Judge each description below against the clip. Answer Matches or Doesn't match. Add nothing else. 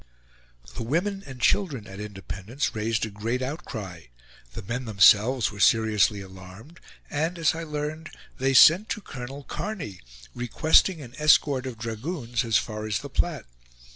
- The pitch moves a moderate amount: Doesn't match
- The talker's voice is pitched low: Matches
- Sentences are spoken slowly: Doesn't match